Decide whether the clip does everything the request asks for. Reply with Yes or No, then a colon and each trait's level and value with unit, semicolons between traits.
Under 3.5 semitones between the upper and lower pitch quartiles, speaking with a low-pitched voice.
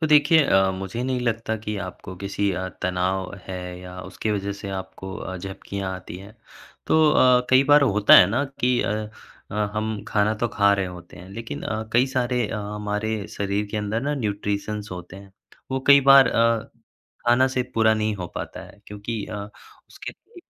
No: average, 3.8 semitones; low, 105 Hz